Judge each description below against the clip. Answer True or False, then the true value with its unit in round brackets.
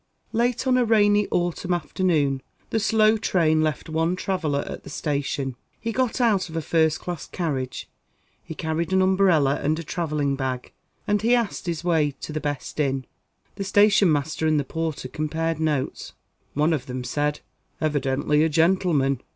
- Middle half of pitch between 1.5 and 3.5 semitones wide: False (4.4 semitones)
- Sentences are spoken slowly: False (170 wpm)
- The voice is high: False (160 Hz)